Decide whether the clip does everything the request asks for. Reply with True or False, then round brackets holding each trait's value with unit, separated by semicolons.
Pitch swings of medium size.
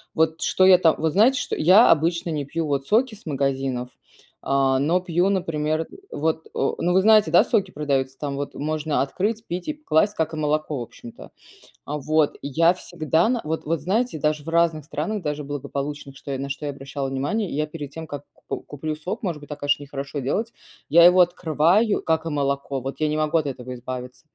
True (3.5 semitones)